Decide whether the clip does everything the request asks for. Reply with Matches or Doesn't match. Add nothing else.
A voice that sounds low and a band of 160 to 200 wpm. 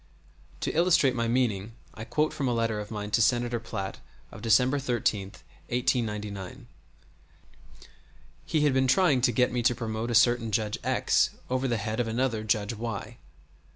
Matches